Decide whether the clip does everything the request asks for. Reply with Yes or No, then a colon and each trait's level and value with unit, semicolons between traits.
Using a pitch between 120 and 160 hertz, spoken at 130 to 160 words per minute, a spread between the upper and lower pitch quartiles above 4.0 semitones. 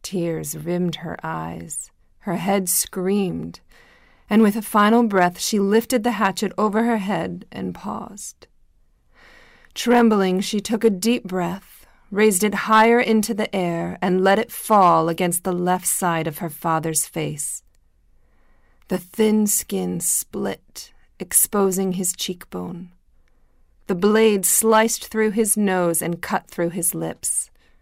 No: medium, 185 Hz; slow, 135 wpm; average, 4.5 semitones